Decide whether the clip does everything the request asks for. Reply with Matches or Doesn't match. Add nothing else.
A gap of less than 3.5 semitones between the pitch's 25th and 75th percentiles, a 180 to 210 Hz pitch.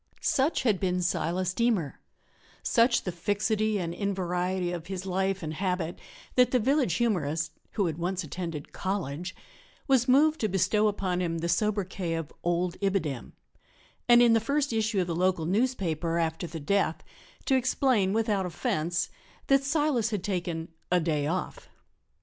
Doesn't match